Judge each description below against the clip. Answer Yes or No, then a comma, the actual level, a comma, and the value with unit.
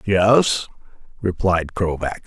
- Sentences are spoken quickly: No, slow, 80 wpm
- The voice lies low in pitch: Yes, very low, 95 Hz